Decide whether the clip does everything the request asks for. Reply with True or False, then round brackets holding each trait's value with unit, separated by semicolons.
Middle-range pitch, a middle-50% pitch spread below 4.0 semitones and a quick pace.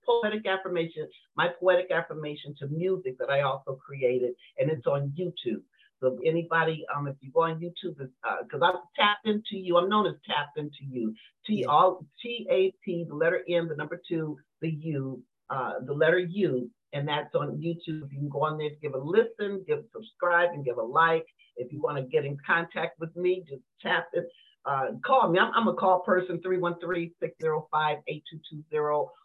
False (165 Hz; 3.6 semitones; 190 wpm)